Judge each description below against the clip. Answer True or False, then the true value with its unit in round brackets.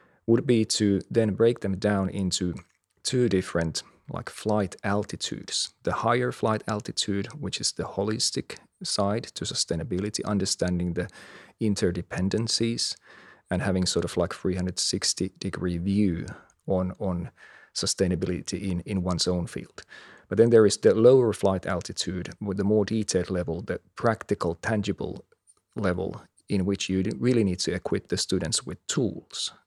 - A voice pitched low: True (95 Hz)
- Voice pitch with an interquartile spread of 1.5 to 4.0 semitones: True (2.9 semitones)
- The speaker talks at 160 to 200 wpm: False (145 wpm)